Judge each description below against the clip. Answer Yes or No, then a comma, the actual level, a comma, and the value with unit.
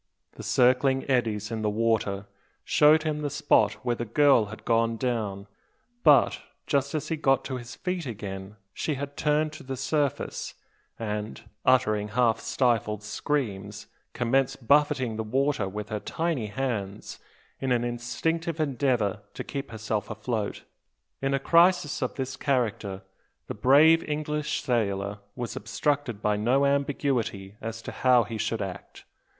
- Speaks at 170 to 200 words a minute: No, average, 150 wpm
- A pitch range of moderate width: Yes, average, 4.8 semitones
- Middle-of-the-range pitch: No, low, 125 Hz